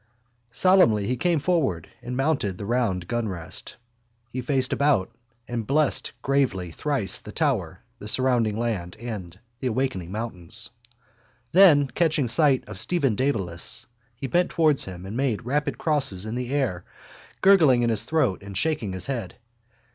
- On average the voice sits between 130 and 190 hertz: No, low, 120 Hz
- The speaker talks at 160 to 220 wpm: No, average, 150 wpm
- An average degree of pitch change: No, wide, 6.0 semitones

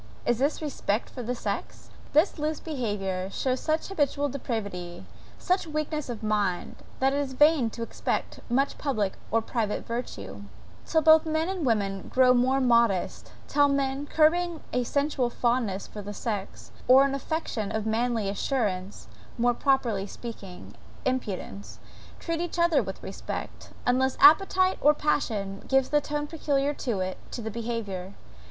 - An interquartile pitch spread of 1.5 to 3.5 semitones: No, wide, 5.5 semitones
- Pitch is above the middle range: Yes, very high, 255 Hz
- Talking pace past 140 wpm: Yes, average, 155 wpm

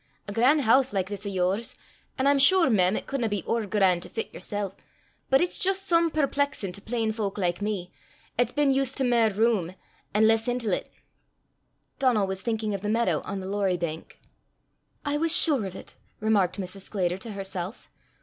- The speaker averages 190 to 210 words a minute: Yes, average, 195 wpm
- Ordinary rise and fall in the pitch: Yes, average, 4.9 semitones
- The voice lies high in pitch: Yes, high, 215 Hz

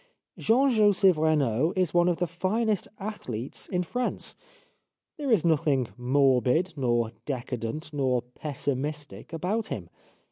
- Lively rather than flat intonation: Yes, wide, 6.4 semitones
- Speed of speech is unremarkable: No, slow, 130 wpm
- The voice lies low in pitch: No, medium, 155 Hz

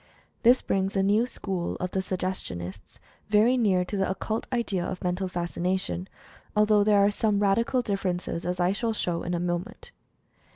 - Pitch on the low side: No, high, 195 Hz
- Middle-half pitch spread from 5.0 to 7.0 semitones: No, average, 2.9 semitones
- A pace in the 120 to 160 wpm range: No, average, 180 wpm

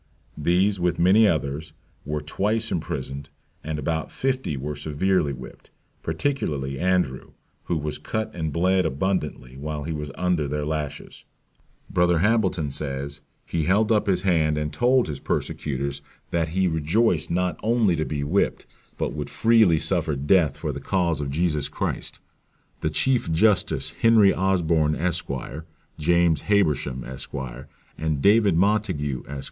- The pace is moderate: Yes, average, 145 wpm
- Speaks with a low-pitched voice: Yes, very low, 80 Hz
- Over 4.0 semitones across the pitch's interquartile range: Yes, average, 4.4 semitones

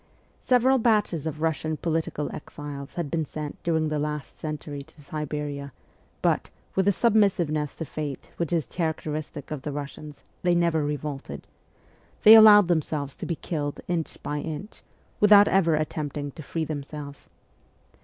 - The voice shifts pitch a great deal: No, narrow, 2.6 semitones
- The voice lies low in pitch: No, medium, 155 Hz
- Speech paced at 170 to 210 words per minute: No, average, 150 wpm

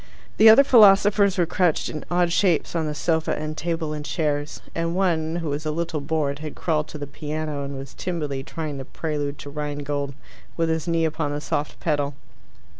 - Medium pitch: Yes, medium, 155 Hz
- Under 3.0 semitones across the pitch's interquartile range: Yes, narrow, 2.4 semitones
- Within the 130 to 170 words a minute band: No, average, 195 wpm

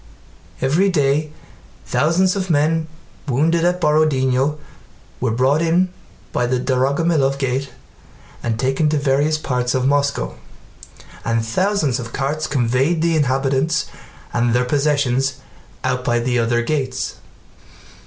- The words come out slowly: Yes, slow, 125 wpm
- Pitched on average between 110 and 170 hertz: Yes, medium, 140 Hz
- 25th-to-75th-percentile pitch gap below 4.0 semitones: Yes, average, 3.6 semitones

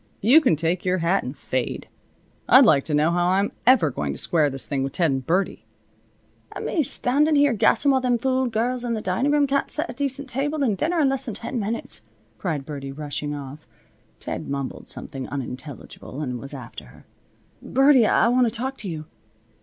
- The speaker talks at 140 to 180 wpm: No, fast, 205 wpm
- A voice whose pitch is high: Yes, high, 195 Hz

